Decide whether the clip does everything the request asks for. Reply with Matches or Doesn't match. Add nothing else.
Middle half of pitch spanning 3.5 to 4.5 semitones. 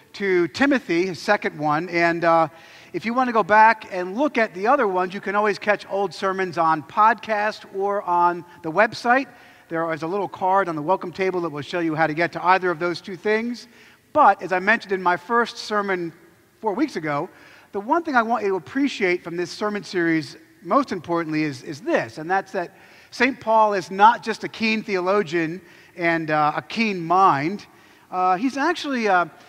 Matches